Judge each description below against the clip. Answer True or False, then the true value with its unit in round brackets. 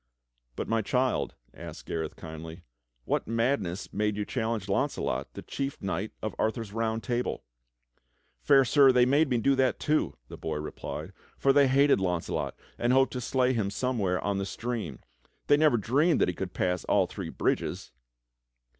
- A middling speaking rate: True (170 wpm)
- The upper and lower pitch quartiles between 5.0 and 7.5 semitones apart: True (5.3 semitones)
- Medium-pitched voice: False (115 Hz)